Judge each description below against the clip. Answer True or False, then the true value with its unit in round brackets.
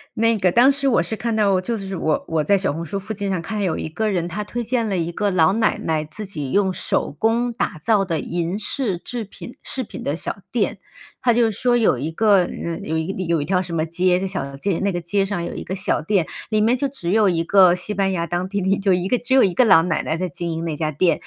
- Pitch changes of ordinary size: True (4.2 semitones)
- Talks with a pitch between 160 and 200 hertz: True (190 Hz)